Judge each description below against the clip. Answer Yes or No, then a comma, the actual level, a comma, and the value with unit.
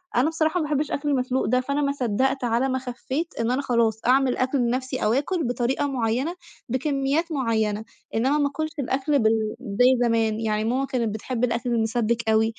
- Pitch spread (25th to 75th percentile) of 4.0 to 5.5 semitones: No, average, 3.5 semitones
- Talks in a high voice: Yes, very high, 255 Hz